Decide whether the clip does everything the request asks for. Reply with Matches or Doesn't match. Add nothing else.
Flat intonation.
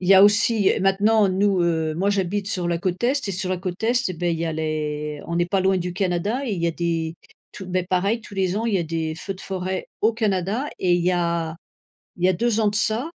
Doesn't match